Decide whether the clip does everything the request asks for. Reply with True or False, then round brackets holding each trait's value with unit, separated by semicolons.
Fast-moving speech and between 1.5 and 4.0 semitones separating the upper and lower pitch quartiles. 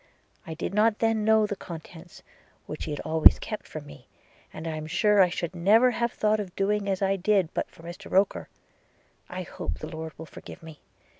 False (220 wpm; 4.4 semitones)